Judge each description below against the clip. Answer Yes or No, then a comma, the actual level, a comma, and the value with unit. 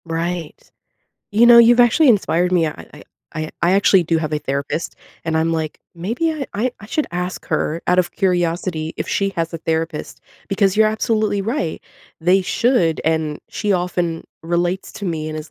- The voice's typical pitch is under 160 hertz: No, medium, 175 Hz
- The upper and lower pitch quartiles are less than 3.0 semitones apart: No, average, 4.0 semitones